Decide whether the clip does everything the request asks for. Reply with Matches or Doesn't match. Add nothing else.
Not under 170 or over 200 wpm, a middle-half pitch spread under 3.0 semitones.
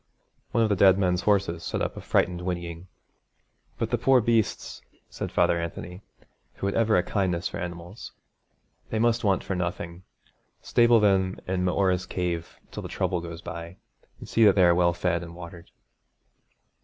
Matches